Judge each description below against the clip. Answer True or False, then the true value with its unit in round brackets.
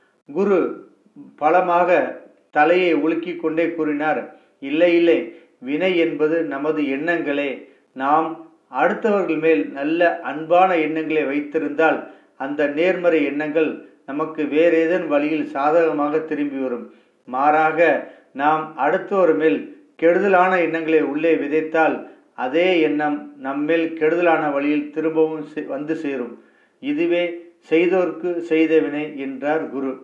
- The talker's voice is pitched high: False (160 Hz)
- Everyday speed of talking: True (100 wpm)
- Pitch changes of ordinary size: False (2.1 semitones)